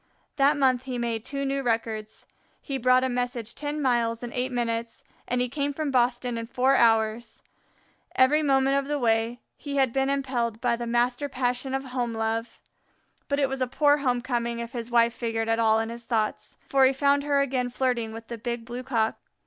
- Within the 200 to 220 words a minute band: Yes, fast, 205 wpm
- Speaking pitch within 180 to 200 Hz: No, high, 245 Hz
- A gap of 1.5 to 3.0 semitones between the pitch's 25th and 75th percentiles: Yes, narrow, 2.6 semitones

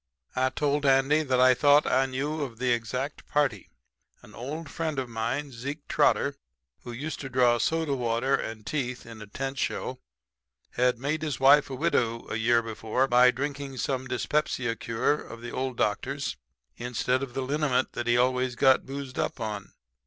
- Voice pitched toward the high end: No, low, 130 Hz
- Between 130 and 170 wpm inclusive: No, average, 180 wpm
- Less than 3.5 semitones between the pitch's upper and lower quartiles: Yes, average, 2.9 semitones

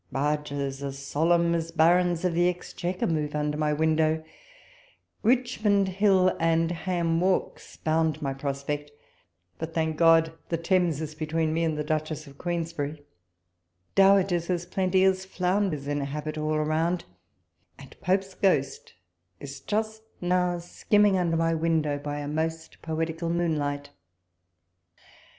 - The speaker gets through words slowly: Yes, slow, 130 wpm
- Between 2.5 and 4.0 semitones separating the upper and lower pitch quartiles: Yes, average, 2.9 semitones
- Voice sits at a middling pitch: Yes, medium, 165 Hz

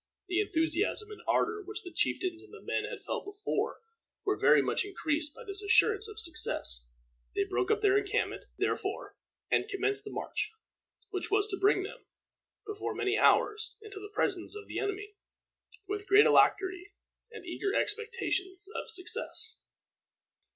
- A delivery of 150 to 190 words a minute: Yes, average, 160 wpm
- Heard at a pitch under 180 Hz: No, very high, 405 Hz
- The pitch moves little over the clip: Yes, narrow, 2.0 semitones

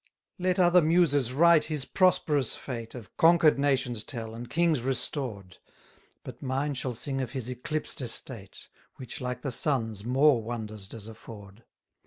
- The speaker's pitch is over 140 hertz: No, low, 130 Hz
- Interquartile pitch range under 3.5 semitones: No, average, 4.5 semitones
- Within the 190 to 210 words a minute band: No, average, 155 wpm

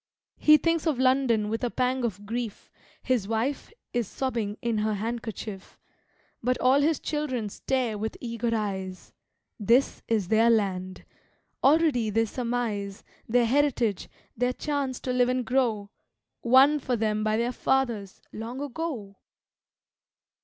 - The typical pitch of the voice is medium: No, high, 235 Hz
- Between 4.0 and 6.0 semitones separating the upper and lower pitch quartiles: No, average, 3.3 semitones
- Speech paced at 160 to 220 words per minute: No, average, 140 wpm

